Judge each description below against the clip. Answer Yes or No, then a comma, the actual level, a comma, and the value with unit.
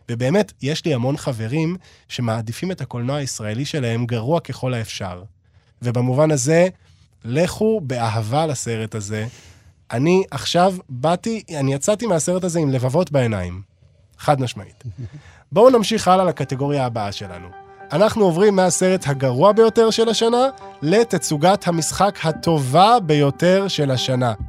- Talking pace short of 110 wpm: No, average, 125 wpm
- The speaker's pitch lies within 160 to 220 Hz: No, medium, 145 Hz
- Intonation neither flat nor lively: No, wide, 7.6 semitones